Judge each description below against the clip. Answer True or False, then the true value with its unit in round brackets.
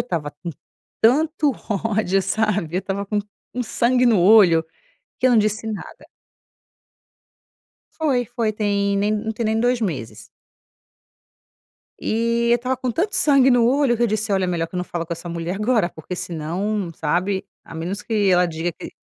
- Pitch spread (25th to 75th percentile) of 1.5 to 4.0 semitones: False (4.9 semitones)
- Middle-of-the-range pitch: False (210 Hz)